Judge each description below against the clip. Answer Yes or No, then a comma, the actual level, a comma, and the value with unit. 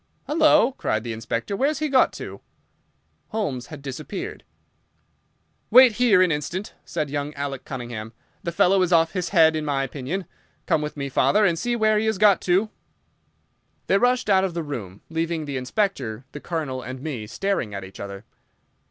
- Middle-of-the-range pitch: Yes, medium, 160 Hz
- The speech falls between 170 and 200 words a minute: Yes, average, 180 wpm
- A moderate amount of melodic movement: No, wide, 7.3 semitones